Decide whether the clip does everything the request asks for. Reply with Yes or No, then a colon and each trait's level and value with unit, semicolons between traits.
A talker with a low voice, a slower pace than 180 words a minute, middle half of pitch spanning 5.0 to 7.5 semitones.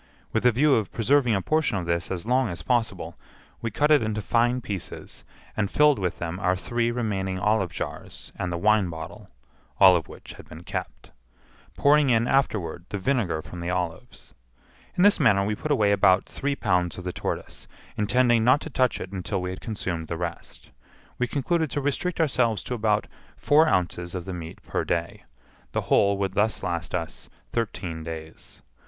No: low, 105 Hz; average, 190 wpm; wide, 5.6 semitones